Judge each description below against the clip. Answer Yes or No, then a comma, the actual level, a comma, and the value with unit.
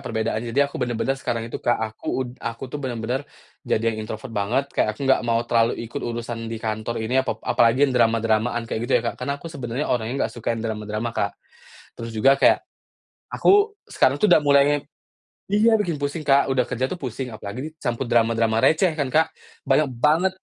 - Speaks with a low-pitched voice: Yes, low, 120 Hz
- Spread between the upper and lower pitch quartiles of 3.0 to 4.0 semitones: Yes, average, 3.6 semitones